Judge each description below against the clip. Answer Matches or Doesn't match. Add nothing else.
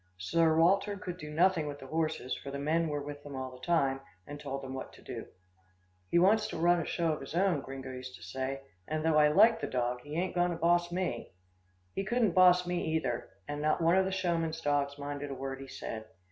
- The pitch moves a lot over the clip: Doesn't match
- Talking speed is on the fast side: Matches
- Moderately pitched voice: Matches